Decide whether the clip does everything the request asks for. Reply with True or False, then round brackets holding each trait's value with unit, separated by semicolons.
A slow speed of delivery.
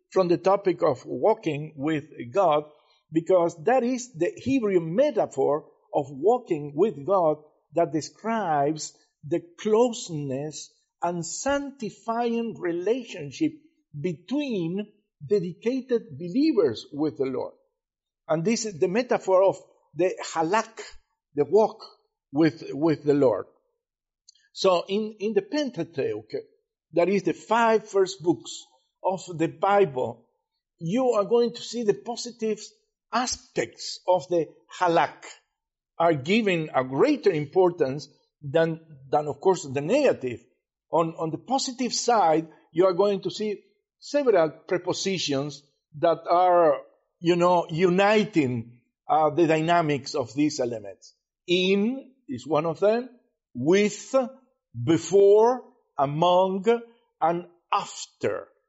True (115 wpm)